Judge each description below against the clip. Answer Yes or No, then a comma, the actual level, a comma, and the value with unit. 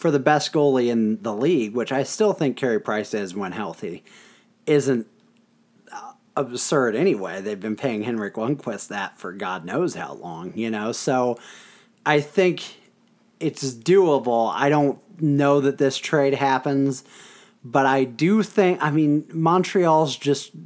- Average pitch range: Yes, average, 4.4 semitones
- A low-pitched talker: No, medium, 145 Hz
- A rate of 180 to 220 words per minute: No, average, 150 wpm